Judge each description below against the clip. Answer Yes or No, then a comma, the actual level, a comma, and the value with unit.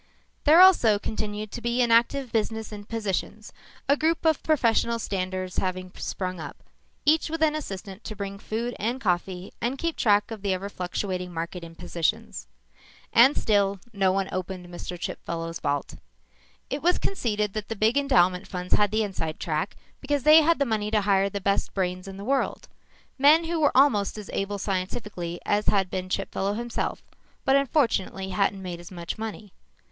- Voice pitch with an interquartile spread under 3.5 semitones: No, average, 4.4 semitones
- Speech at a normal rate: Yes, average, 175 wpm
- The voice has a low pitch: No, high, 205 Hz